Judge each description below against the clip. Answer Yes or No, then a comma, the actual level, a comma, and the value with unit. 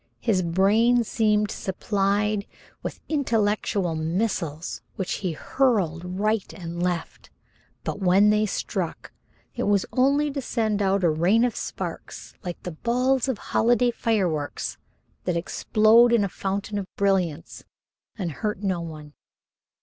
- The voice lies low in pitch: No, high, 200 Hz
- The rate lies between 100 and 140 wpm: Yes, slow, 135 wpm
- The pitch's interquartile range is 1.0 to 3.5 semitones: No, average, 4.1 semitones